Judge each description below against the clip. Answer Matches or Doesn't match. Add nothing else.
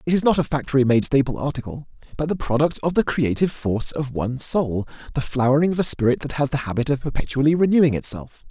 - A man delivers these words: Matches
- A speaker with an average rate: Doesn't match